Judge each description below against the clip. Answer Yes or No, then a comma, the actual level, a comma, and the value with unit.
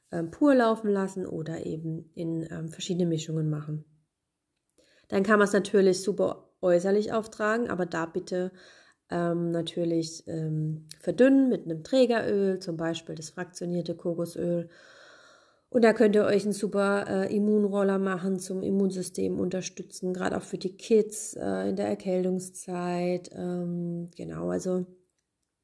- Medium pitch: Yes, medium, 180 Hz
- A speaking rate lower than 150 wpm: Yes, average, 135 wpm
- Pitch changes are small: No, average, 3.2 semitones